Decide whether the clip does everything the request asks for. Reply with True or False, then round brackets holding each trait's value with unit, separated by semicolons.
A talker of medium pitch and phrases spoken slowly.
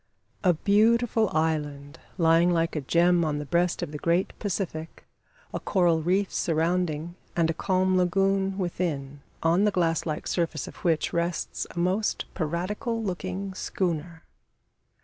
False (175 Hz; 145 wpm)